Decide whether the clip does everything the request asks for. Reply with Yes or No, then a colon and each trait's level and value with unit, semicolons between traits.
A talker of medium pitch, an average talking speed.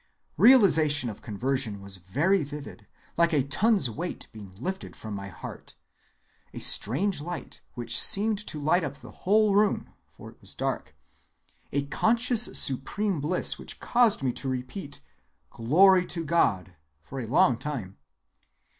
Yes: medium, 145 Hz; average, 145 wpm